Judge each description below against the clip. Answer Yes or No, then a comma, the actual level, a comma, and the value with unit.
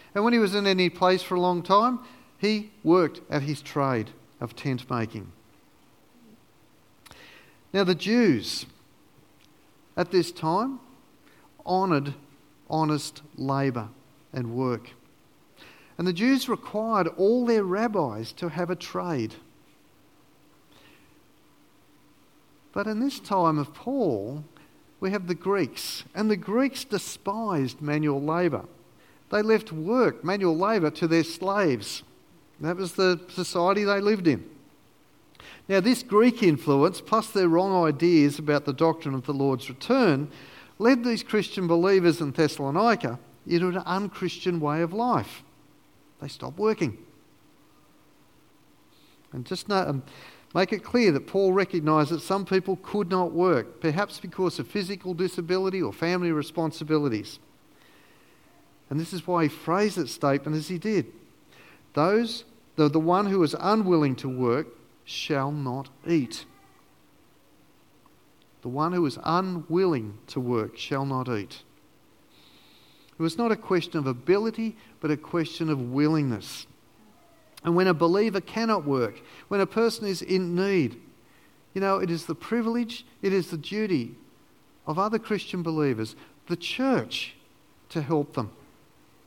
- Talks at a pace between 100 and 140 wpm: Yes, slow, 135 wpm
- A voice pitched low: No, medium, 170 Hz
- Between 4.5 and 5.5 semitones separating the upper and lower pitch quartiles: Yes, average, 5.2 semitones